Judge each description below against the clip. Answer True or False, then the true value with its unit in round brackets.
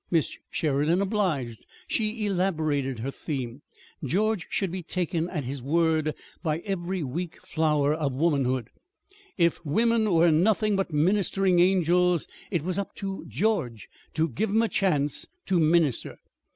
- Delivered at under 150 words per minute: True (140 wpm)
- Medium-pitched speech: True (170 Hz)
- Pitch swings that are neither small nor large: True (4.6 semitones)